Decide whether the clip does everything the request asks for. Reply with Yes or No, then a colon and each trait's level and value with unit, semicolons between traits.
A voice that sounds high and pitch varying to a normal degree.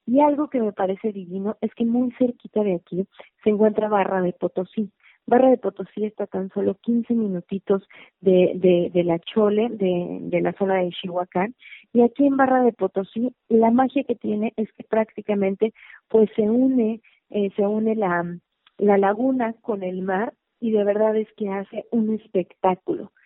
Yes: high, 210 Hz; average, 3.2 semitones